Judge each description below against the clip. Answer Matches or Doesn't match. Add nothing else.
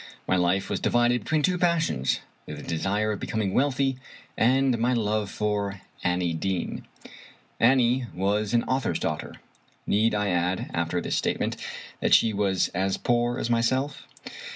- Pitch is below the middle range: Matches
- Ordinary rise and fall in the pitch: Matches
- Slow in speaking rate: Doesn't match